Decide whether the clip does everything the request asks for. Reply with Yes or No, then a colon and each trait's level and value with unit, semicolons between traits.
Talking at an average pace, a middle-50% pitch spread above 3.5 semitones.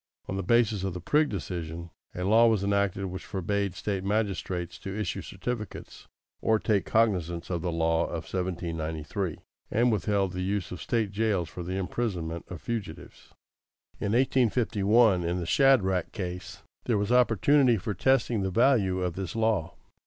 Yes: average, 160 wpm; average, 3.9 semitones